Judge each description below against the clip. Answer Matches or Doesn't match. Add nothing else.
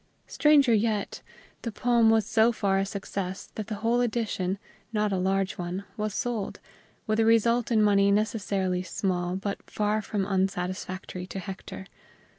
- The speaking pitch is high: Matches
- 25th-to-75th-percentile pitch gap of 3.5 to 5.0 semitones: Doesn't match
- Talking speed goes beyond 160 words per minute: Doesn't match